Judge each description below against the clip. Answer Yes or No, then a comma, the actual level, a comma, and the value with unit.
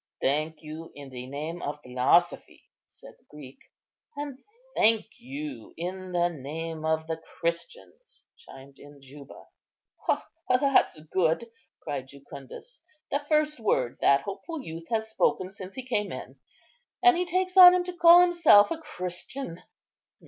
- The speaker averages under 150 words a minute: Yes, average, 140 wpm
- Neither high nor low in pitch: Yes, medium, 180 Hz